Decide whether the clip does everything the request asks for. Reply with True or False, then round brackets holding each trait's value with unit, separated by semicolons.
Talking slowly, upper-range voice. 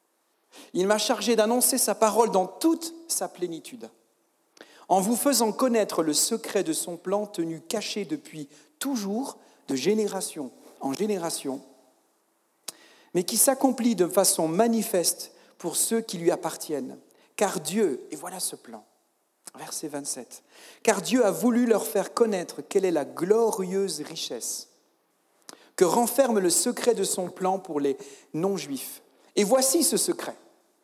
True (140 wpm; 210 Hz)